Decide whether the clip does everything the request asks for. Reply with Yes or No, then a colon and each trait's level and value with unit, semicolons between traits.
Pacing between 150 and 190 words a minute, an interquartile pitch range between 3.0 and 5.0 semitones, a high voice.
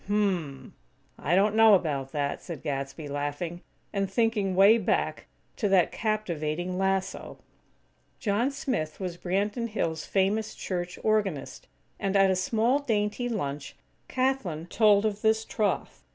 No: average, 140 wpm; average, 4.5 semitones; high, 195 Hz